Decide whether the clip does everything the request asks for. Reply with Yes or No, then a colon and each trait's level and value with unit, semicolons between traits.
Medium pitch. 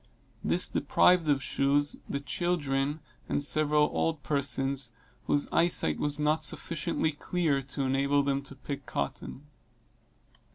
Yes: medium, 145 Hz